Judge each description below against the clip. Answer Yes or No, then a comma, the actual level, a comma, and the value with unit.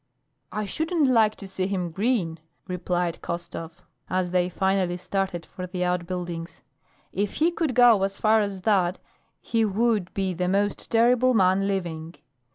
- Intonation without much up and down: No, average, 3.3 semitones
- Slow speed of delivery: No, average, 155 wpm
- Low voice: No, high, 190 Hz